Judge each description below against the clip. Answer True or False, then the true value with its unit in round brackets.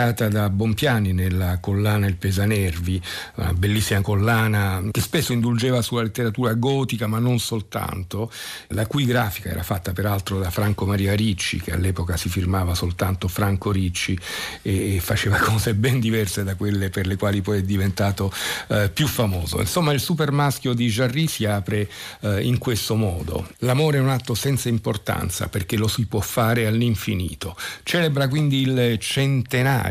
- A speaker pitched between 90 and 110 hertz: True (105 Hz)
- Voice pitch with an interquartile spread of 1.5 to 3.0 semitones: False (3.6 semitones)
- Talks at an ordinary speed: True (160 wpm)